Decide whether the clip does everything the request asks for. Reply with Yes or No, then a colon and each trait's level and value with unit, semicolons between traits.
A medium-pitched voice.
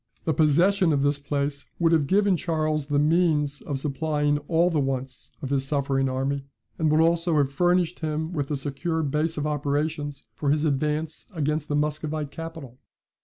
Yes: medium, 150 Hz